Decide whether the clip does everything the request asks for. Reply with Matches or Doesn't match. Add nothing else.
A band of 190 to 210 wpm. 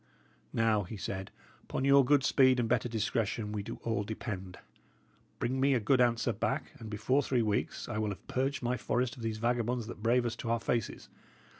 Matches